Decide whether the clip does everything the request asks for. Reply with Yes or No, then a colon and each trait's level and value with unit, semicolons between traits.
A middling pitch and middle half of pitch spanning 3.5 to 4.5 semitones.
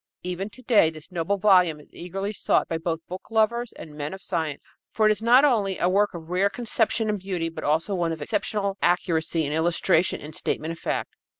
Yes: medium, 180 Hz; average, 4.1 semitones